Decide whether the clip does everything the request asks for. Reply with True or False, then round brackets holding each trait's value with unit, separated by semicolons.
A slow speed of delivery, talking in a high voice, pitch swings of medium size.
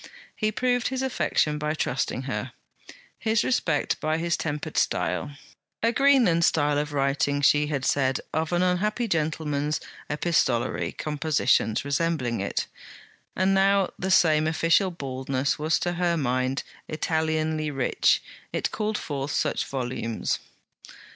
False (130 wpm; 155 Hz; 4.0 semitones)